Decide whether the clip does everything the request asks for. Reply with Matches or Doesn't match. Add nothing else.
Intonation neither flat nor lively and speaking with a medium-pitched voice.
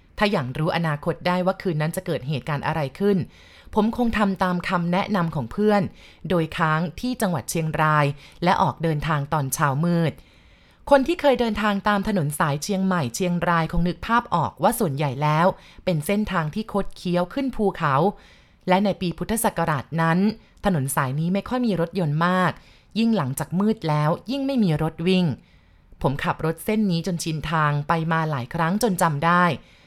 Matches